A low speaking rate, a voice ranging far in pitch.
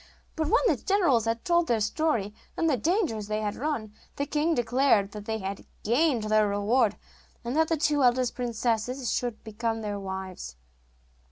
No: average, 175 wpm; wide, 5.7 semitones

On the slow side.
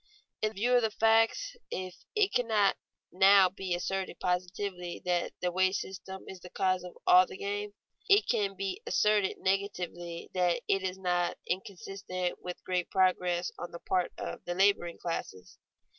No: average, 160 wpm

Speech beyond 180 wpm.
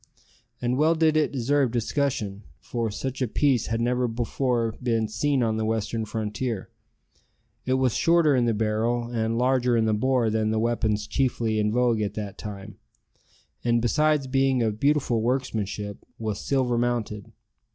No: average, 160 wpm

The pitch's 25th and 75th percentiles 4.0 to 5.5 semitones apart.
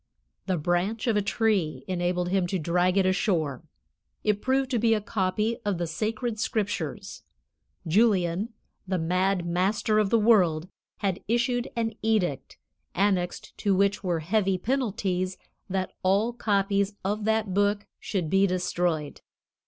No: average, 3.3 semitones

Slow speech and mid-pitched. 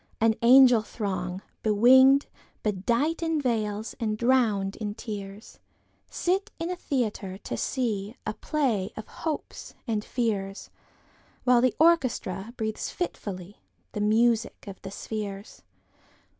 No: slow, 100 wpm; high, 220 Hz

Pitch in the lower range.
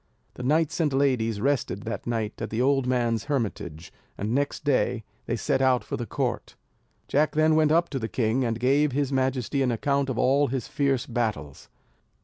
Yes: low, 130 Hz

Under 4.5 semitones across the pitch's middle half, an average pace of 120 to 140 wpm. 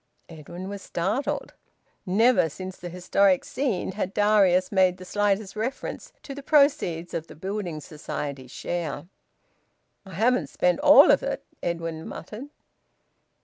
Yes: average, 3.9 semitones; slow, 135 wpm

